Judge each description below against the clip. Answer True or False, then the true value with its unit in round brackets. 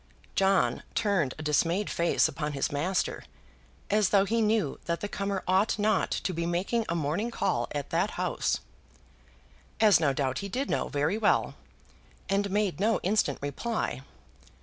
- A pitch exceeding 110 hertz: True (190 Hz)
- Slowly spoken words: False (160 wpm)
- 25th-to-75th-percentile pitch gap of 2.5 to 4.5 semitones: False (5.0 semitones)